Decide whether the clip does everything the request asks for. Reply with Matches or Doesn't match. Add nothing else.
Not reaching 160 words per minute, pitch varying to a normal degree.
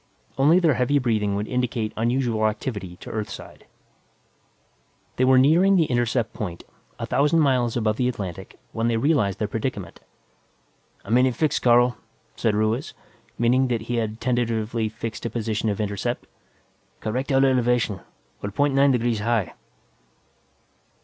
Matches